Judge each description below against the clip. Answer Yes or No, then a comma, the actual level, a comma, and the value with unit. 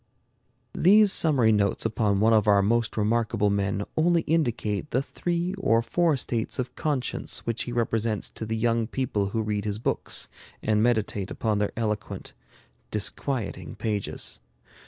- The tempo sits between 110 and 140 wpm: No, average, 150 wpm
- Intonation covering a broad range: No, average, 3.4 semitones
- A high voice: No, low, 115 Hz